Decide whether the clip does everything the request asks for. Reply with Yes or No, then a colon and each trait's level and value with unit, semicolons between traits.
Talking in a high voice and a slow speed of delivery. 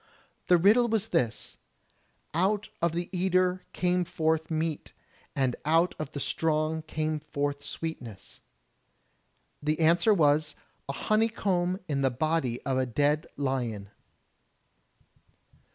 No: medium, 155 Hz; slow, 120 wpm